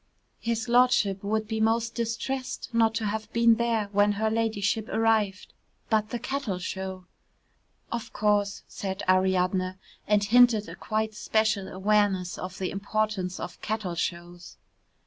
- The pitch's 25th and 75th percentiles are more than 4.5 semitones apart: No, average, 2.8 semitones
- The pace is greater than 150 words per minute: No, average, 145 wpm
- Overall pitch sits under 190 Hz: No, high, 215 Hz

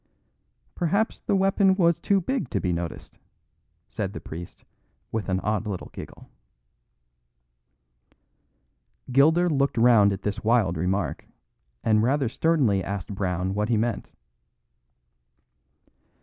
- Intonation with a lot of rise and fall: Yes, wide, 8.6 semitones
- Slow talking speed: Yes, slow, 120 wpm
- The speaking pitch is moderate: No, low, 110 Hz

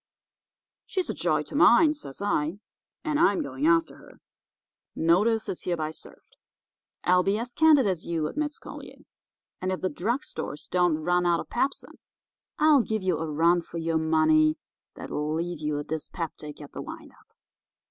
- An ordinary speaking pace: Yes, average, 170 wpm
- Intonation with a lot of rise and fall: Yes, wide, 7.0 semitones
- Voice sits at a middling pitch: Yes, medium, 175 Hz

